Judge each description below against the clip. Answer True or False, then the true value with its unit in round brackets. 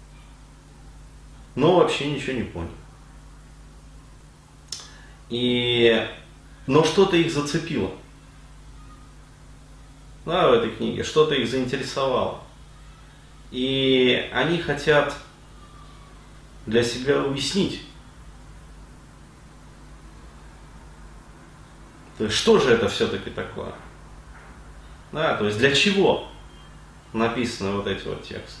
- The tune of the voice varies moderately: False (8.7 semitones)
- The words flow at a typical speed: False (85 wpm)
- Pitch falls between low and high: False (120 Hz)